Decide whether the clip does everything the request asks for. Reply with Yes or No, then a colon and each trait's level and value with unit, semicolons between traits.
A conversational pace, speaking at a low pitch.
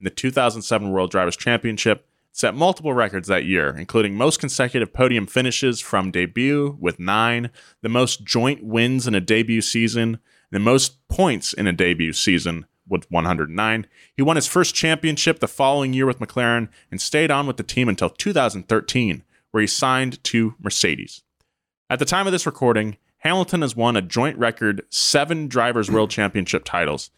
Yes: average, 170 wpm; low, 120 Hz